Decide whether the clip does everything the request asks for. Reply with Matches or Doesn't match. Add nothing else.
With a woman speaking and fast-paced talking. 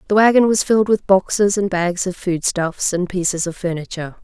Matches